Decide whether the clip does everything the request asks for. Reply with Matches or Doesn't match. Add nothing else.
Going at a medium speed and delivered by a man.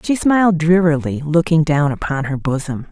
Doesn't match